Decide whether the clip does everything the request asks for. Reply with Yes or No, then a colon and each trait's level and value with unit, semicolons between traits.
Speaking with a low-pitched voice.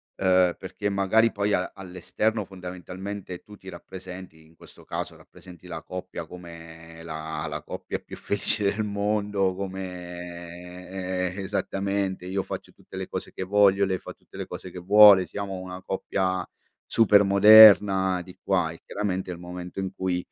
Yes: very low, 95 Hz